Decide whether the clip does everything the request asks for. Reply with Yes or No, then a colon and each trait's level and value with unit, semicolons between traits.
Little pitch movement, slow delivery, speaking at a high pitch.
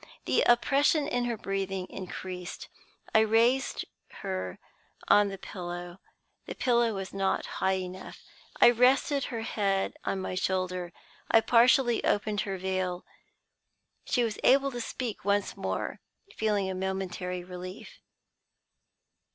No: average, 4.2 semitones; slow, 125 wpm; high, 195 Hz